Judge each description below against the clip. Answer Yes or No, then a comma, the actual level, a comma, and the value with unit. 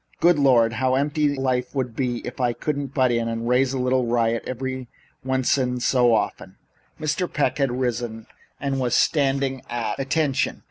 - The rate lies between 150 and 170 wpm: No, average, 180 wpm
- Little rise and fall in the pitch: Yes, narrow, 2.1 semitones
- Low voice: Yes, low, 130 Hz